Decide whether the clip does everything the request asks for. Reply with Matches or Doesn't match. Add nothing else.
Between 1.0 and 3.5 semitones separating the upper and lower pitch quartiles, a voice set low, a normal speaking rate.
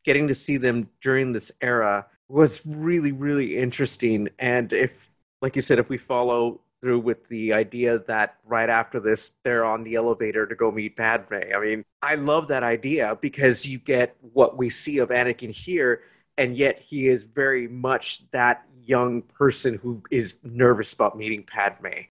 Matches